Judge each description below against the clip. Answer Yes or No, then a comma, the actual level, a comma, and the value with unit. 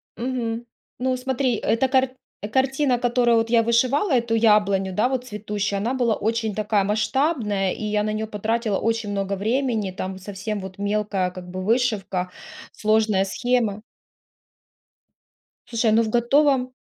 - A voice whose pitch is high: Yes, high, 220 Hz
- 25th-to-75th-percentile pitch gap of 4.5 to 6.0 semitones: No, average, 3.3 semitones